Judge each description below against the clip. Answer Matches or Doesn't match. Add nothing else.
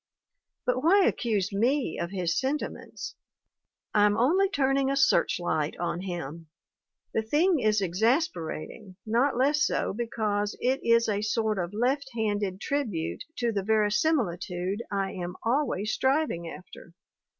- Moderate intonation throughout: Doesn't match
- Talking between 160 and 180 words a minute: Doesn't match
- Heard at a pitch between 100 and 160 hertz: Doesn't match